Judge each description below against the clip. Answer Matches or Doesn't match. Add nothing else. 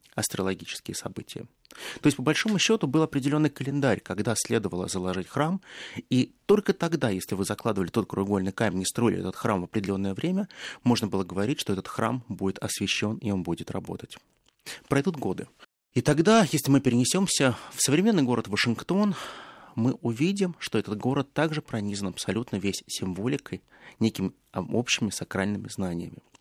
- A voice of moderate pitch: Doesn't match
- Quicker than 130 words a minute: Matches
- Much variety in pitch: Matches